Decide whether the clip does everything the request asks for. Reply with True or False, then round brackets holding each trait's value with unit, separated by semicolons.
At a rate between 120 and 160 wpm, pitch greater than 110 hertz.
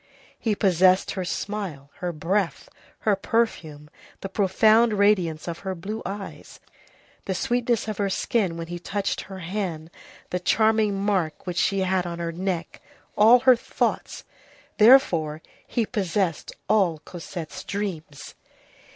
True (135 wpm; 190 Hz)